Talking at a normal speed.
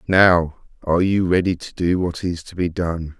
Yes: average, 190 wpm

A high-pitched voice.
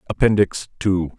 No: very low, 95 Hz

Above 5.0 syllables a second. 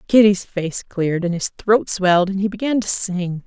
No: 4.6 syllables/s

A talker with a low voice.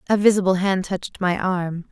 No: medium, 185 Hz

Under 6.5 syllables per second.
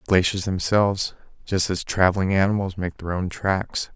Yes: 5.0 syllables/s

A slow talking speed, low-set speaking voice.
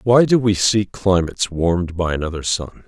No: average, 190 wpm; very low, 95 Hz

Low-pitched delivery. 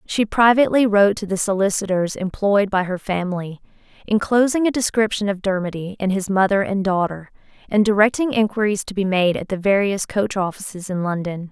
No: high, 200 Hz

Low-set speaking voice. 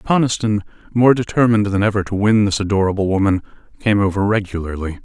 Yes: low, 105 Hz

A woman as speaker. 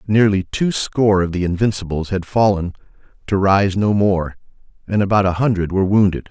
No: male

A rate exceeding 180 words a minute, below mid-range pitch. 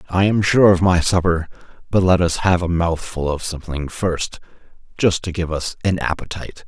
Yes: average, 190 wpm; very low, 85 Hz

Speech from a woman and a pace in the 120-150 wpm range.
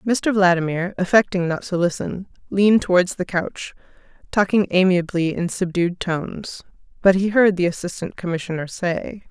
Yes: female; average, 140 wpm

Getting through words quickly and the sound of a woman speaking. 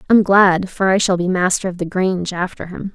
Yes: fast, 245 wpm; female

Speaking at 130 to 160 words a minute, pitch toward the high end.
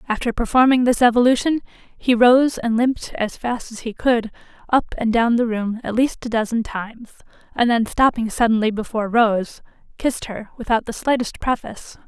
No: average, 175 wpm; high, 235 Hz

